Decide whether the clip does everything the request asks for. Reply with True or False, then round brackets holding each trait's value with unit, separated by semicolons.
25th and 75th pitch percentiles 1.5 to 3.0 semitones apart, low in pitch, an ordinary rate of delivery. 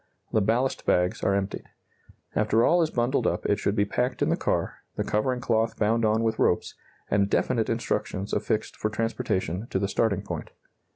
True (2.7 semitones; 110 Hz; 185 wpm)